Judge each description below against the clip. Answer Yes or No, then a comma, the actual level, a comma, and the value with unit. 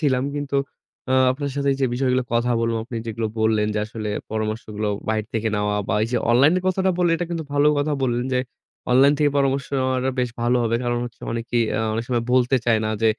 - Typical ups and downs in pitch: Yes, average, 3.4 semitones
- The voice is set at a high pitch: No, low, 125 Hz